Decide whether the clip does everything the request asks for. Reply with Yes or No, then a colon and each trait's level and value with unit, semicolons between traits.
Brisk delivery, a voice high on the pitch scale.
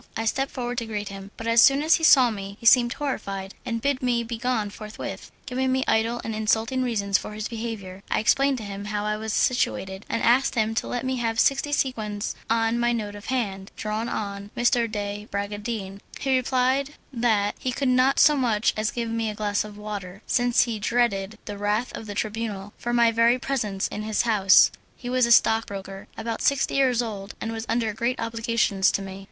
Yes: fast, 210 wpm; high, 225 Hz